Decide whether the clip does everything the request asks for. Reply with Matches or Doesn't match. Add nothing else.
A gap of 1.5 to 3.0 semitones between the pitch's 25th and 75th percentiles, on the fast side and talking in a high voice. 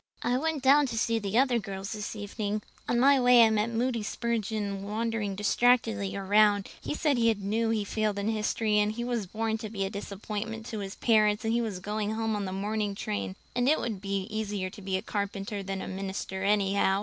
Matches